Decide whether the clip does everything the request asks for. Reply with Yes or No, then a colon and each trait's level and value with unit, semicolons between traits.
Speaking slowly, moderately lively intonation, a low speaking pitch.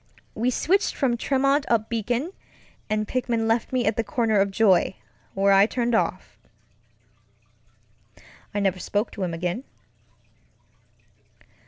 No: slow, 130 wpm; average, 3.7 semitones; high, 225 Hz